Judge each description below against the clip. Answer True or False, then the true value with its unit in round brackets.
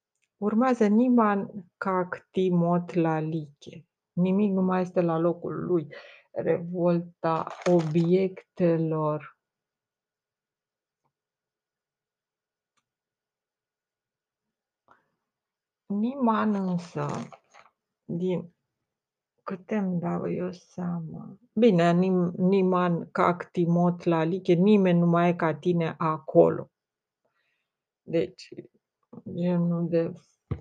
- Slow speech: True (75 wpm)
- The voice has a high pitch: False (175 Hz)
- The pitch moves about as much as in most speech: False (2.1 semitones)